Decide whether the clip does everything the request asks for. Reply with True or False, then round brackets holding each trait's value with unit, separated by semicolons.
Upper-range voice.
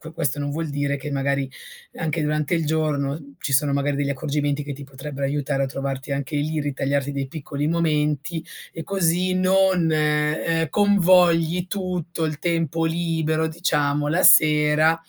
False (150 Hz)